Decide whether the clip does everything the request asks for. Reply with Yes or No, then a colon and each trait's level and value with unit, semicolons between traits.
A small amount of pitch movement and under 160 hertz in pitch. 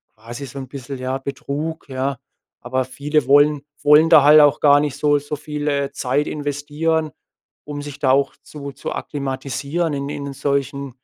Yes: narrow, 1.4 semitones; medium, 140 Hz